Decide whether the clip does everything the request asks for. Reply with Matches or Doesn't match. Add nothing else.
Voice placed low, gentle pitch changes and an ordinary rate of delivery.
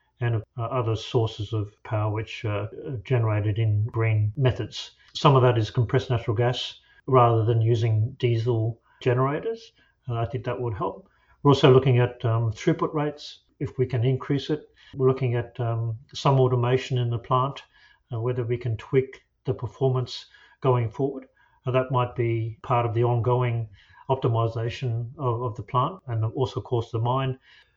Matches